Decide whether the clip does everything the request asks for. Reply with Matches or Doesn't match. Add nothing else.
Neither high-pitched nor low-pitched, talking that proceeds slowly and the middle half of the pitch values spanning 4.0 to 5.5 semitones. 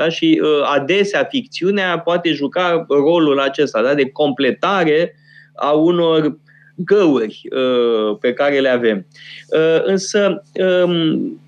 Matches